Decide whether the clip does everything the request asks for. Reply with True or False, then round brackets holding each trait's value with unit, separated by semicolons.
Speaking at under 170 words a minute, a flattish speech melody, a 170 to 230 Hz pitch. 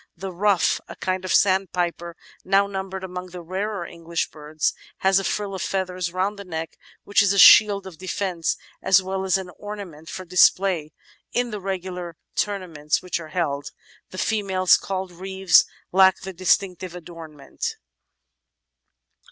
True (150 wpm; 2.1 semitones; 185 Hz)